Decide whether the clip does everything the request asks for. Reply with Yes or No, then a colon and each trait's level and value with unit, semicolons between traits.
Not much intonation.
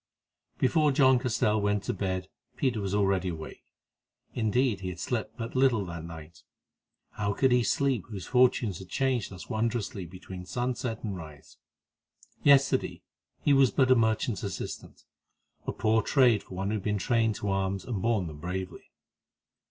No: average, 4.7 semitones